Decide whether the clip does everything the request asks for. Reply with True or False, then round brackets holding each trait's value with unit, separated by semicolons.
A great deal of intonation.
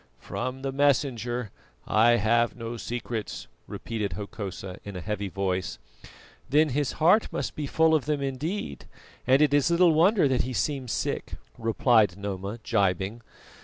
True (5.8 semitones)